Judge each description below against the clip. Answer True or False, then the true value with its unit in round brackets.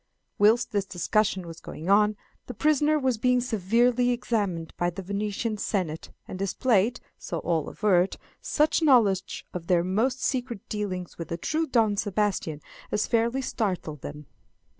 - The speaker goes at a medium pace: True (150 wpm)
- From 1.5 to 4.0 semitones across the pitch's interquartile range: False (5.1 semitones)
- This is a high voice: True (210 Hz)